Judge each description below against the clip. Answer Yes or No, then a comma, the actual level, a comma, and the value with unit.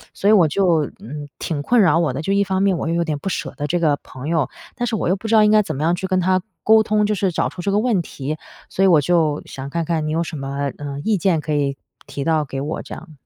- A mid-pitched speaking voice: Yes, medium, 165 Hz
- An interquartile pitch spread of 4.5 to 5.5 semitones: Yes, average, 4.8 semitones